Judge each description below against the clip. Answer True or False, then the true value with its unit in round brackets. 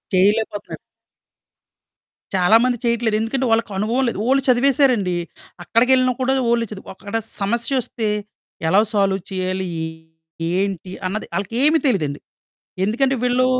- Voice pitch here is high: True (225 Hz)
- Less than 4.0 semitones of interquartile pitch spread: False (4.4 semitones)